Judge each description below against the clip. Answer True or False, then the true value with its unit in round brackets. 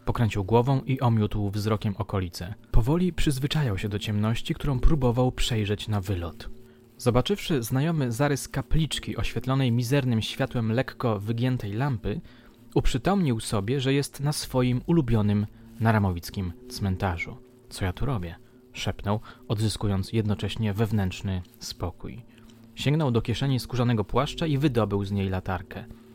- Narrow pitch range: False (3.8 semitones)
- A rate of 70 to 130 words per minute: True (125 wpm)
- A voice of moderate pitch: False (120 Hz)